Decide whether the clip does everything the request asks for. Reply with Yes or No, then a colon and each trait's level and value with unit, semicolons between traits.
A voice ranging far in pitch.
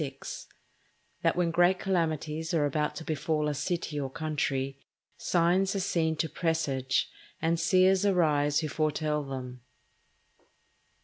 No: average, 2.8 semitones